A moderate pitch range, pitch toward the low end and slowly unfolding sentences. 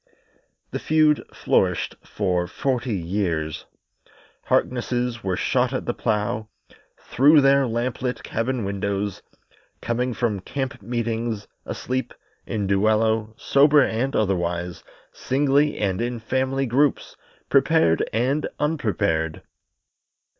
Yes: average, 4.6 semitones; low, 115 Hz; slow, 105 wpm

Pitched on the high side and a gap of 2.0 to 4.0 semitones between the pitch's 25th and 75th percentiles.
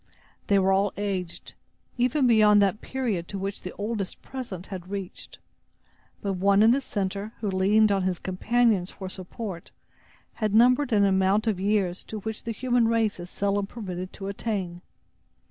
Yes: high, 200 Hz; average, 2.8 semitones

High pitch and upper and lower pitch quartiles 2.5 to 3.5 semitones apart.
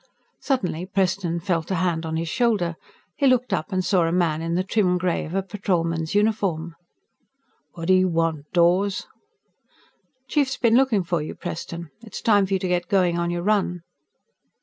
No: medium, 180 Hz; average, 3.1 semitones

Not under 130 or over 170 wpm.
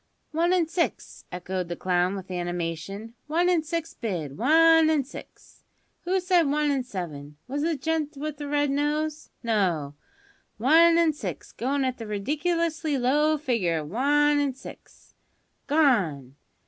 Yes: average, 155 wpm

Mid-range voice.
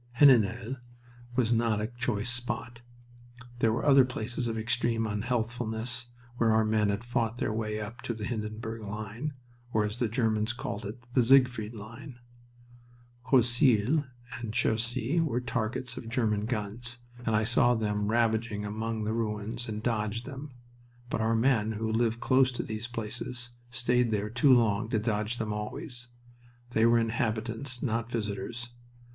No: low, 115 Hz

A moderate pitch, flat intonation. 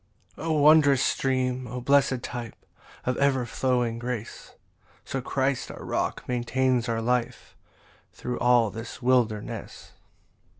No: low, 125 Hz; narrow, 1.7 semitones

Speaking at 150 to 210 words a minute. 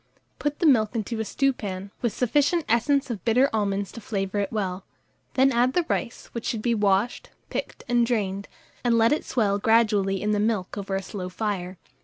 Yes: average, 195 wpm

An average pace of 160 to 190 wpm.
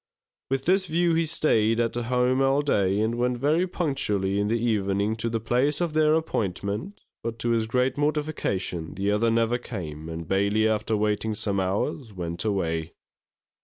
Yes: average, 170 wpm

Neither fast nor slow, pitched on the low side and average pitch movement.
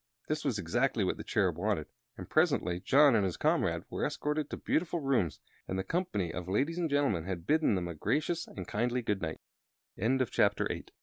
No: average, 185 wpm; low, 120 Hz; wide, 8.2 semitones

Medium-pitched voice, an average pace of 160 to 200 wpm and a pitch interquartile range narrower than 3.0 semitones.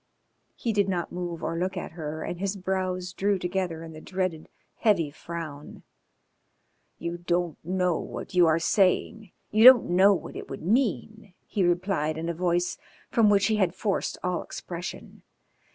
Yes: medium, 180 Hz; average, 170 wpm; narrow, 2.5 semitones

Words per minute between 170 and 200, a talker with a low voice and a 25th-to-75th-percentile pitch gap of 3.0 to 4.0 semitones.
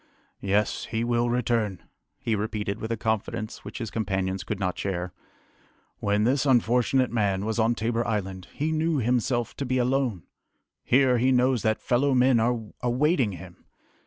No: average, 160 wpm; low, 115 Hz; average, 3.3 semitones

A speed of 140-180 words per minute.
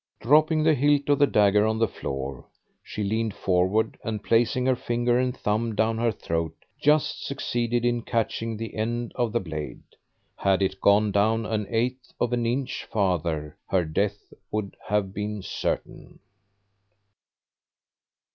Yes: average, 150 wpm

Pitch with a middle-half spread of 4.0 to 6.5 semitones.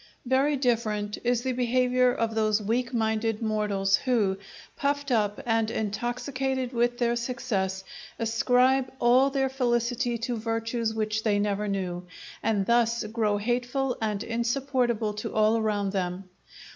No: average, 2.7 semitones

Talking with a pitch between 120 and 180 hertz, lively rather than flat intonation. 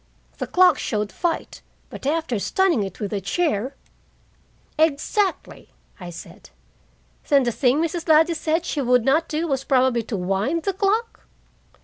No: very high, 285 Hz; wide, 6.2 semitones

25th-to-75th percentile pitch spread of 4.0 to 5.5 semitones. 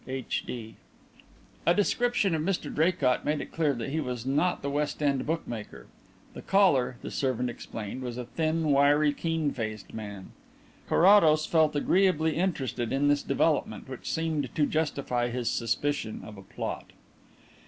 Yes: average, 4.5 semitones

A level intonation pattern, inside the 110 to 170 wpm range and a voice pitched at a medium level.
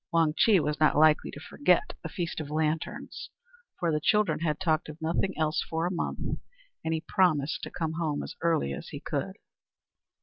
No: narrow, 1.8 semitones; average, 195 wpm; medium, 160 Hz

